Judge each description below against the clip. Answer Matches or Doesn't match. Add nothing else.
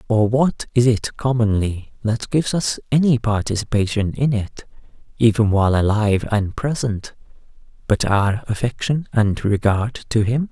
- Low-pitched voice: Matches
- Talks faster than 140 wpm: Doesn't match